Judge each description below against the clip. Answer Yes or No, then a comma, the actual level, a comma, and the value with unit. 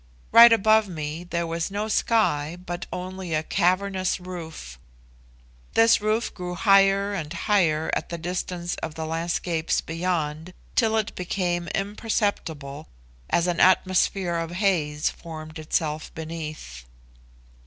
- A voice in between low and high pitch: Yes, medium, 175 Hz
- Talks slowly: Yes, slow, 125 wpm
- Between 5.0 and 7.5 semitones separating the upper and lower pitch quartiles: No, average, 3.4 semitones